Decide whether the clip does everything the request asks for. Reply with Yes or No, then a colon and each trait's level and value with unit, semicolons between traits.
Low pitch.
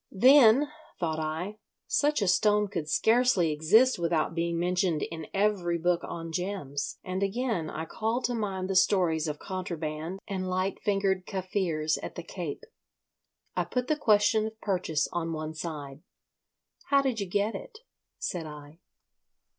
No: medium, 185 Hz